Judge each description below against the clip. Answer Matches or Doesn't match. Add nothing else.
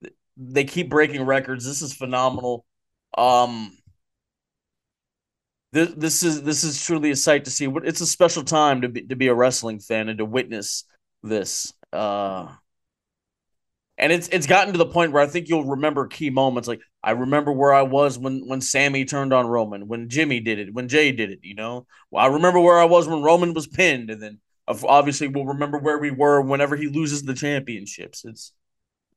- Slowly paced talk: Doesn't match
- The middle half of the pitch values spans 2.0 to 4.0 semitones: Matches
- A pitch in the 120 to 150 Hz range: Matches